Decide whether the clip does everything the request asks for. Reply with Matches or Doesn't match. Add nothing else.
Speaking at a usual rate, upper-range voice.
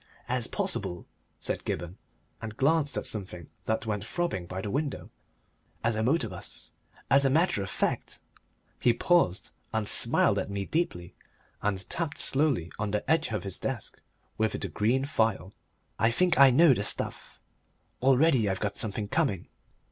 Doesn't match